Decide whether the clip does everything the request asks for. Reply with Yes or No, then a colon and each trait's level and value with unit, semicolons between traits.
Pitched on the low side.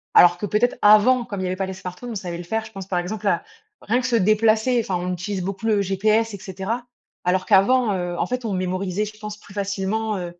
No: high, 200 Hz